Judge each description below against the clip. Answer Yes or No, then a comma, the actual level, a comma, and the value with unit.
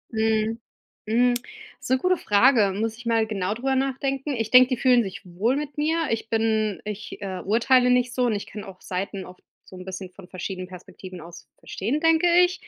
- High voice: Yes, high, 225 Hz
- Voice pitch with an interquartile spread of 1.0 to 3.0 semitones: No, average, 4.8 semitones